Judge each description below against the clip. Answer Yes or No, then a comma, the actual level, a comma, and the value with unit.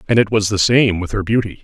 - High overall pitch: No, low, 105 Hz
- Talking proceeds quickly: Yes, fast, 295 wpm